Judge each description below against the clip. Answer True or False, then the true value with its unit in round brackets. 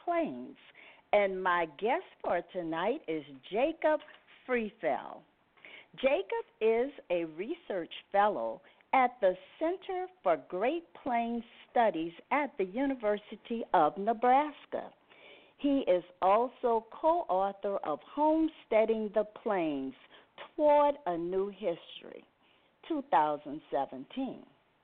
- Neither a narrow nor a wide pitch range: False (7.5 semitones)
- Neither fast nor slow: False (95 wpm)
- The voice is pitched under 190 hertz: False (240 Hz)